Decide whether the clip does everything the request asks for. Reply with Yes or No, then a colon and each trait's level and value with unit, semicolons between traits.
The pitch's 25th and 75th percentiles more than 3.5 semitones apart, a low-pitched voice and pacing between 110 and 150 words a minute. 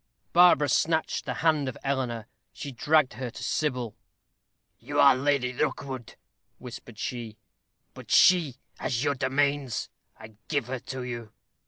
No: average, 3.0 semitones; low, 130 Hz; average, 140 wpm